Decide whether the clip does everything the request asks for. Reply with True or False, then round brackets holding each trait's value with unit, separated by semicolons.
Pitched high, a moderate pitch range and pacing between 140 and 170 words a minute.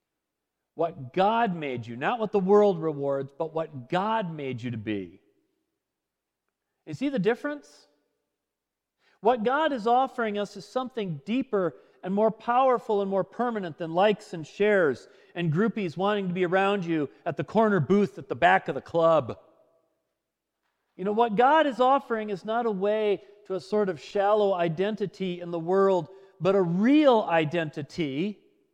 True (200 Hz; 4.9 semitones; 165 wpm)